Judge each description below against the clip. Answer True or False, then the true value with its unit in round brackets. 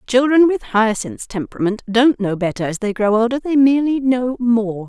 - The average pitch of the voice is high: True (235 Hz)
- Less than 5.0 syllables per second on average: False (5.1 syllables/s)